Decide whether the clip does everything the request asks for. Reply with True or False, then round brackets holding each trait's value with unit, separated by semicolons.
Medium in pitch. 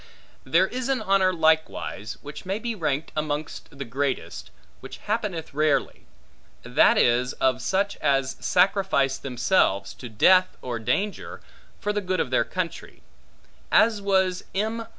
True (165 Hz)